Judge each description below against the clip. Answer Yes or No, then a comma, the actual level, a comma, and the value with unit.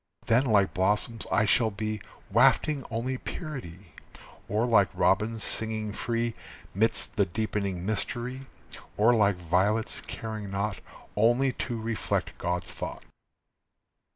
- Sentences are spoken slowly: Yes, slow, 120 wpm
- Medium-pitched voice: No, low, 110 Hz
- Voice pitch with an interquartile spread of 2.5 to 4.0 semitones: Yes, average, 2.8 semitones